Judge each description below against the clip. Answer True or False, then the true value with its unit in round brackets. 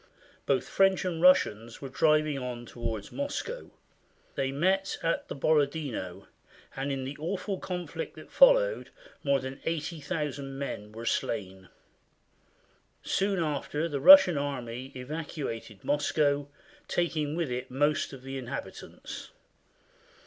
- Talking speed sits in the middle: False (125 wpm)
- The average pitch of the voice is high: False (145 Hz)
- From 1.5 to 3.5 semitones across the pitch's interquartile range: False (4.3 semitones)